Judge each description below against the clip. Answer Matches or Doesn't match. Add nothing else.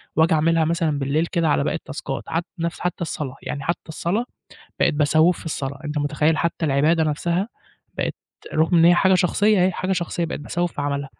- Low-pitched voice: Doesn't match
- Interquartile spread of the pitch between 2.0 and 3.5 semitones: Matches